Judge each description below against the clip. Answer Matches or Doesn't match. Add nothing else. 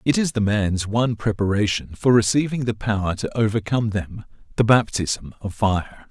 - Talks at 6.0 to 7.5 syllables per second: Doesn't match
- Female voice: Doesn't match